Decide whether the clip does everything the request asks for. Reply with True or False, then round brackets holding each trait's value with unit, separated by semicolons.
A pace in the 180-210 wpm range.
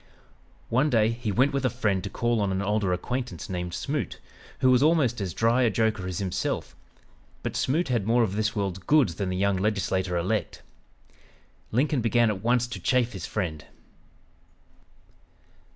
False (170 wpm)